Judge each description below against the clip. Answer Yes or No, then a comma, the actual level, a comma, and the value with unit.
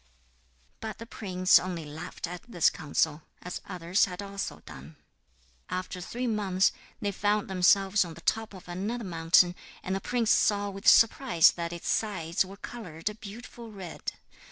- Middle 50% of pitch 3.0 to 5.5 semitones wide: Yes, average, 3.3 semitones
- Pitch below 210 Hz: Yes, high, 190 Hz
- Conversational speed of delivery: Yes, average, 160 wpm